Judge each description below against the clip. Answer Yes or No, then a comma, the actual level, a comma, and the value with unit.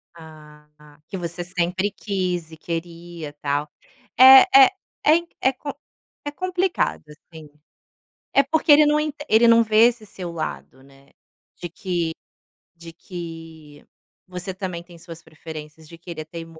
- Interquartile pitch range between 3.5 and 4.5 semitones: No, wide, 5.4 semitones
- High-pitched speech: No, medium, 170 Hz